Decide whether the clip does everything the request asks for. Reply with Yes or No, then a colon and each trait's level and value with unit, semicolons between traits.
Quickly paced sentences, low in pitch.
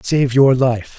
No: average, 185 wpm; low, 130 Hz